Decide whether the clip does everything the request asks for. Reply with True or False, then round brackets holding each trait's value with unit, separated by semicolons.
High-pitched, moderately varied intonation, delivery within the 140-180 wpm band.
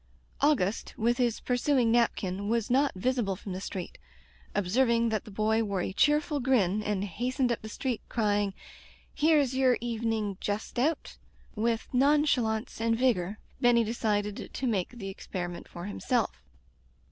True (225 Hz; 3.5 semitones; 155 wpm)